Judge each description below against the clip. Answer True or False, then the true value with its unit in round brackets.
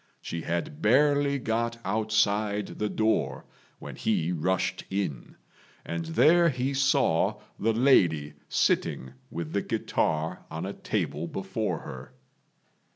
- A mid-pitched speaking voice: False (105 Hz)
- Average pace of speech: False (120 wpm)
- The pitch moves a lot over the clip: True (6.2 semitones)